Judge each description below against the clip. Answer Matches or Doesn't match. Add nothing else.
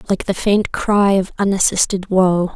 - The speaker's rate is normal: Matches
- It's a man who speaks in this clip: Doesn't match